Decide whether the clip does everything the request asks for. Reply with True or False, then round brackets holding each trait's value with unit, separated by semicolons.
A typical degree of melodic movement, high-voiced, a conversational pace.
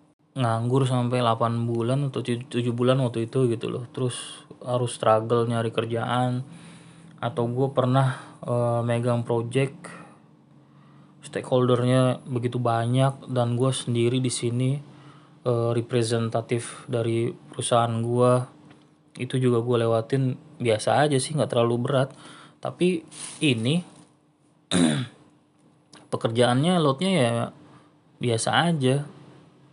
False (3.7 semitones; 125 Hz; 105 wpm)